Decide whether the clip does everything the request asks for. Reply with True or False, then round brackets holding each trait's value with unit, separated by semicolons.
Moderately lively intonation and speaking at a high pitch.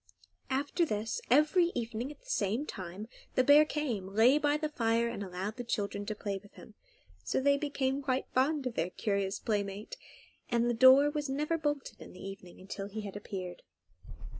False (6.1 semitones; 235 Hz)